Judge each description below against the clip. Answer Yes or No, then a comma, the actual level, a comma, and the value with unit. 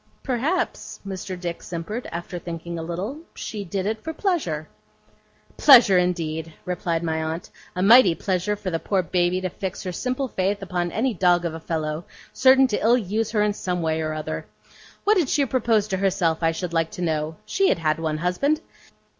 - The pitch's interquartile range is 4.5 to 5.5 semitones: Yes, average, 4.8 semitones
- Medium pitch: Yes, medium, 180 Hz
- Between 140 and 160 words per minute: No, average, 195 wpm